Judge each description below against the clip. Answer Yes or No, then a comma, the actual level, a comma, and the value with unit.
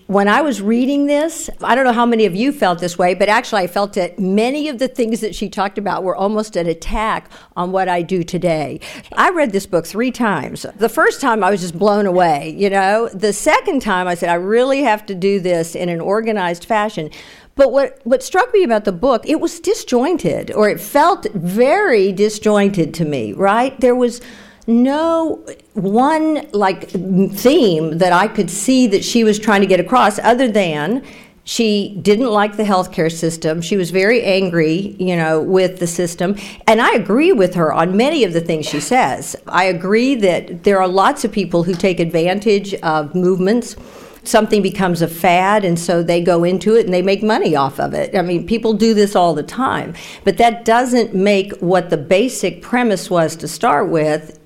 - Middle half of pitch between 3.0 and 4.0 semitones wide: No, average, 4.4 semitones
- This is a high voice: Yes, high, 200 Hz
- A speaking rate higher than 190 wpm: Yes, average, 200 wpm